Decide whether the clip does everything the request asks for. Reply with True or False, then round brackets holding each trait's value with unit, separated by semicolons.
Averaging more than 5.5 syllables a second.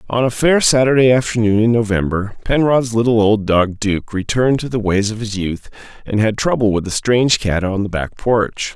False (5.2 syllables/s)